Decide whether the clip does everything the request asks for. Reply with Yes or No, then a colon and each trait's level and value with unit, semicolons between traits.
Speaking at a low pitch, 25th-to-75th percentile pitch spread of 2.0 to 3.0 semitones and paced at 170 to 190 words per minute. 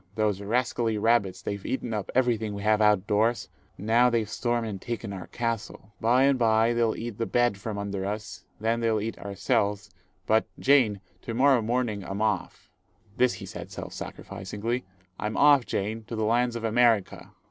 Yes: low, 110 Hz; narrow, 2.5 semitones; average, 180 wpm